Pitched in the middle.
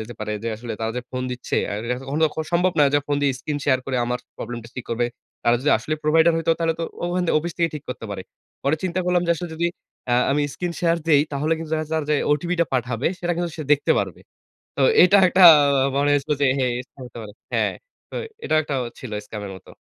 Yes: medium, 145 Hz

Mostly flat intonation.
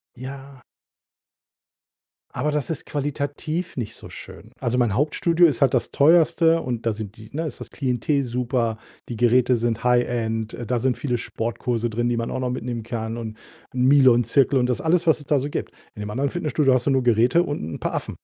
No: average, 3.6 semitones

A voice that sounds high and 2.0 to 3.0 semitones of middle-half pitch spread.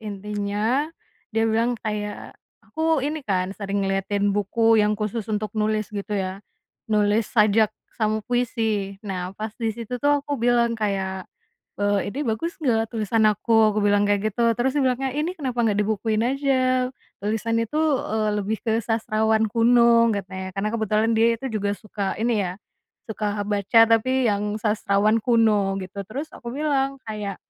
Yes: high, 220 Hz; narrow, 2.5 semitones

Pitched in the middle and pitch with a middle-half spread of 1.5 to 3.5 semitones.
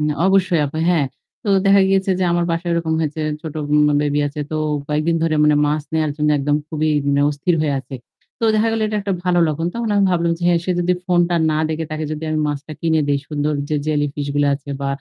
Yes: medium, 155 Hz; average, 2.8 semitones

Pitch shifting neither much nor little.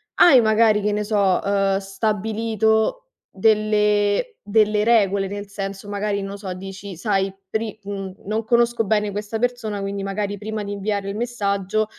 No: narrow, 1.6 semitones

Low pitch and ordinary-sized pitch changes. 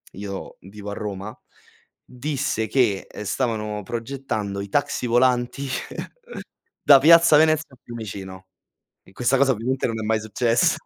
Yes: low, 115 Hz; average, 4.4 semitones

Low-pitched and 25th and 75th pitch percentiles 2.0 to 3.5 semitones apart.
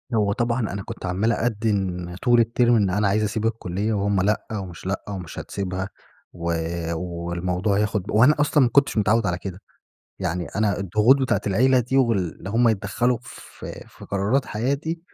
No: low, 105 Hz; average, 3.9 semitones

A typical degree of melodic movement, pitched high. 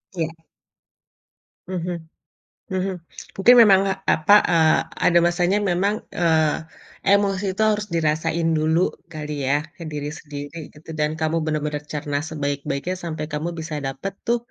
No: average, 3.1 semitones; medium, 160 Hz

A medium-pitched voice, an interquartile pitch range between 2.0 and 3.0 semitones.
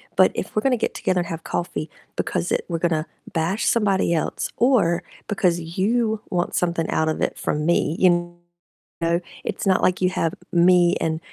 Yes: medium, 175 Hz; narrow, 2.4 semitones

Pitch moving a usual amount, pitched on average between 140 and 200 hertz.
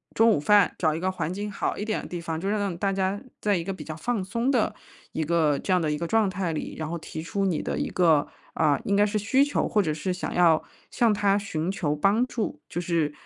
Yes: average, 4.1 semitones; medium, 185 Hz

